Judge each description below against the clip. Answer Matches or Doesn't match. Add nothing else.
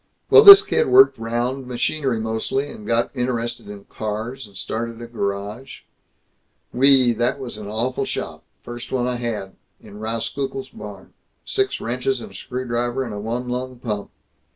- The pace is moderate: Matches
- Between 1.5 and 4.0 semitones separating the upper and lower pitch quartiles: Matches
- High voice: Doesn't match